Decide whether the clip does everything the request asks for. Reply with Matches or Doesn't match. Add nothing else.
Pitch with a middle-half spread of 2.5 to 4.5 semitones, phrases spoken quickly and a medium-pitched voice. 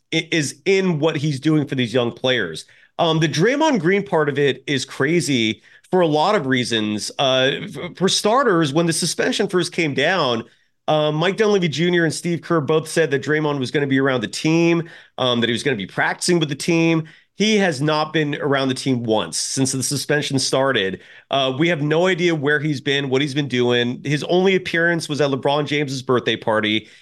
Matches